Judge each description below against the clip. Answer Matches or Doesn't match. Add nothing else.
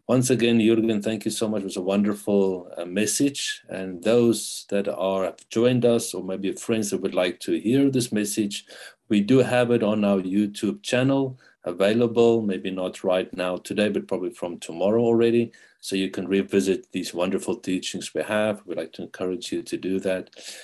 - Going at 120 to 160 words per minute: Doesn't match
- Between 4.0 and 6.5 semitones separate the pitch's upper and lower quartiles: Doesn't match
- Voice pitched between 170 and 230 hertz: Doesn't match